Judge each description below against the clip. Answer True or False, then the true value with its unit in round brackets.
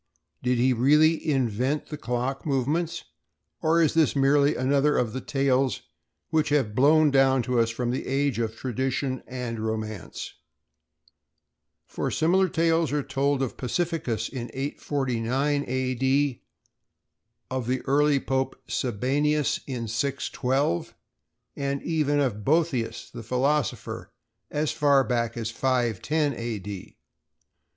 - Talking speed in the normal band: False (130 wpm)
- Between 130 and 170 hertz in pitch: True (135 Hz)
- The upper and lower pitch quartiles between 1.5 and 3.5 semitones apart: True (3.1 semitones)